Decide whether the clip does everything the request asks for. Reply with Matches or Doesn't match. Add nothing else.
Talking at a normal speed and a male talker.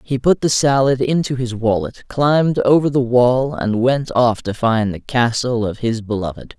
Matches